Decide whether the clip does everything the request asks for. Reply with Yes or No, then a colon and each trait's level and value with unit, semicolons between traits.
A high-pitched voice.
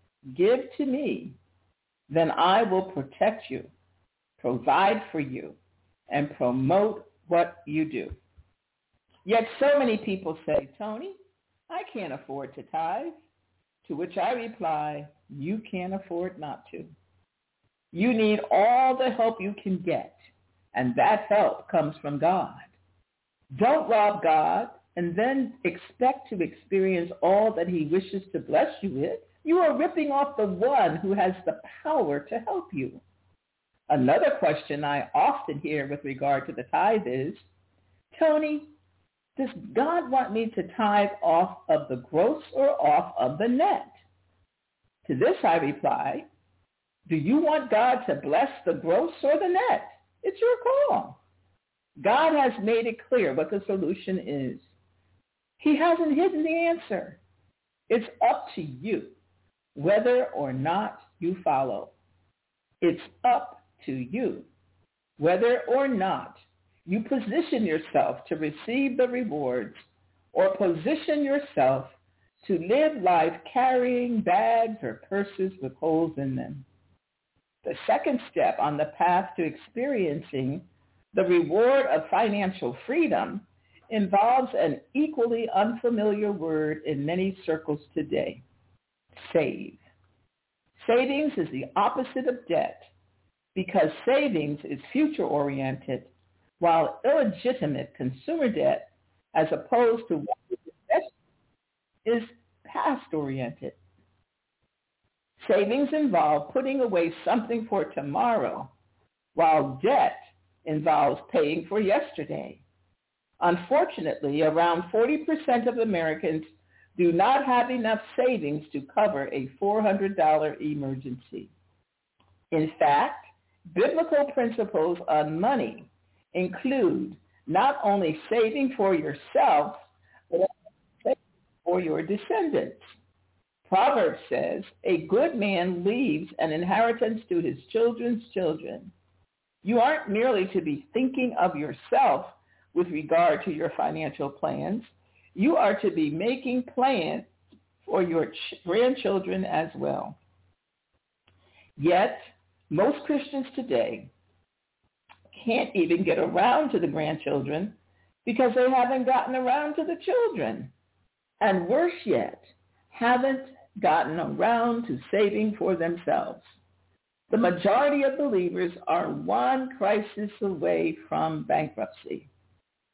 Yes: high, 205 Hz